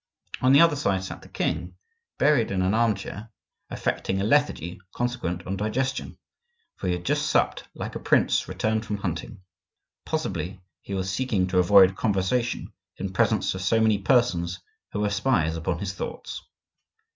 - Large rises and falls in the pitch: No, average, 4.6 semitones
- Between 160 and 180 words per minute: Yes, average, 165 wpm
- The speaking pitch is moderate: No, low, 100 Hz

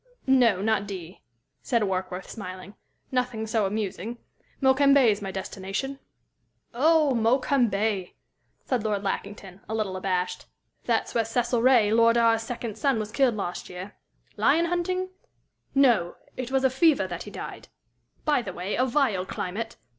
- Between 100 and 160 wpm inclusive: Yes, average, 145 wpm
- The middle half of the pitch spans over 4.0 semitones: Yes, average, 4.9 semitones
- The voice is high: Yes, high, 225 Hz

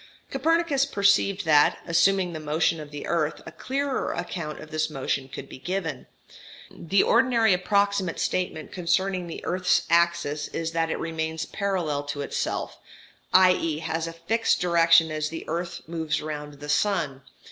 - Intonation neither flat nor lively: Yes, average, 3.7 semitones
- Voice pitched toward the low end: No, medium, 165 Hz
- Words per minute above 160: No, average, 155 wpm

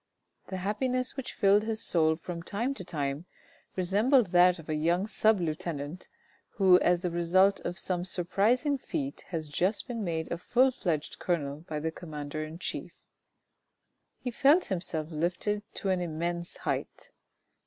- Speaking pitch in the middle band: Yes, medium, 180 Hz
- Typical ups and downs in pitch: Yes, average, 4.4 semitones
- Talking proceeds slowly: No, average, 160 wpm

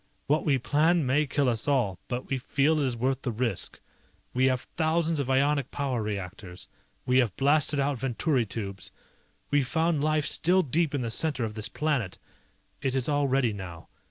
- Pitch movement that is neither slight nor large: Yes, average, 4.0 semitones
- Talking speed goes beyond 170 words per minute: Yes, average, 185 wpm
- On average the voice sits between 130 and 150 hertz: Yes, low, 135 Hz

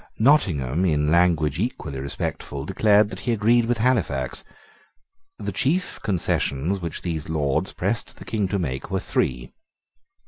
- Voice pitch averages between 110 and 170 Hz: No, very low, 85 Hz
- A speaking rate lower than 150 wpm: Yes, average, 140 wpm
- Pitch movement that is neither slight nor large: No, wide, 6.9 semitones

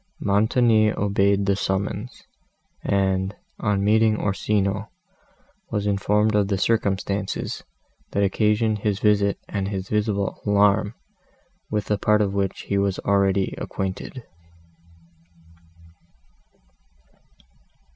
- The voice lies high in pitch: No, low, 100 Hz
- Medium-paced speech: No, slow, 100 wpm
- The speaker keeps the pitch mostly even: Yes, narrow, 1.3 semitones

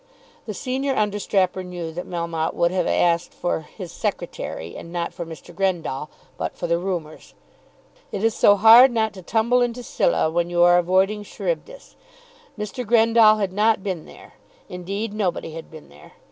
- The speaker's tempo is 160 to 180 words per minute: Yes, average, 170 wpm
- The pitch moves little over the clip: No, average, 4.2 semitones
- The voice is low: No, high, 190 Hz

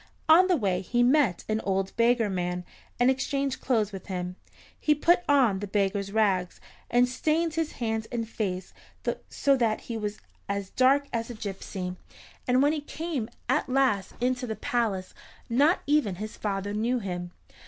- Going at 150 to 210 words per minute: Yes, average, 170 wpm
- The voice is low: No, high, 225 Hz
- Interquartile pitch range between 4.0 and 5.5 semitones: Yes, average, 5.1 semitones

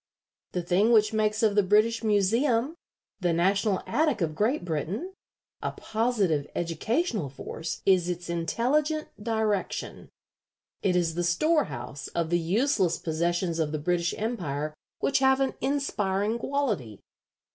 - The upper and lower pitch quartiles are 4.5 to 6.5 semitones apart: Yes, wide, 5.4 semitones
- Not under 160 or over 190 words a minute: No, slow, 135 wpm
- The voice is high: Yes, high, 200 Hz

